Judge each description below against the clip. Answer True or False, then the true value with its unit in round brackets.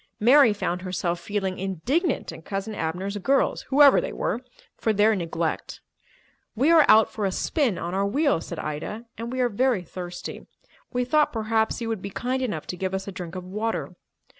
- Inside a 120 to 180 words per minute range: False (190 wpm)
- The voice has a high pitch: True (210 Hz)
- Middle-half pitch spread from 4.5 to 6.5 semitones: True (5.1 semitones)